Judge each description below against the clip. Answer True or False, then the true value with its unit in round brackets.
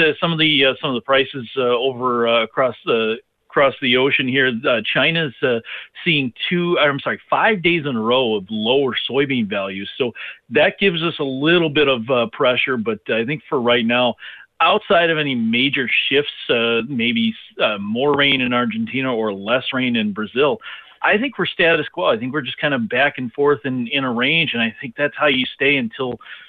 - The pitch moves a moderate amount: True (4.2 semitones)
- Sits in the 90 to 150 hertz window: True (135 Hz)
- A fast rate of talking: True (210 wpm)